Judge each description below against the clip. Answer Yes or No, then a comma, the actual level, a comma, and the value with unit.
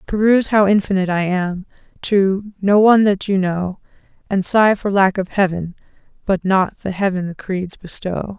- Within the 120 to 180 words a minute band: Yes, average, 170 wpm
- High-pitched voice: Yes, high, 195 Hz